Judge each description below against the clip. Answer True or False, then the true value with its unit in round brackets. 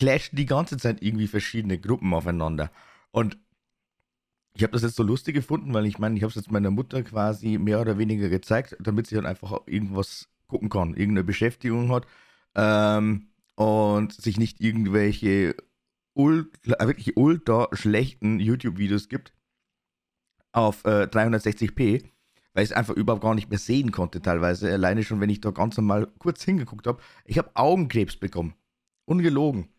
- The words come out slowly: False (160 wpm)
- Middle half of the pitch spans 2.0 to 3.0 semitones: True (2.6 semitones)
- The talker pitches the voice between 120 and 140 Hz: False (110 Hz)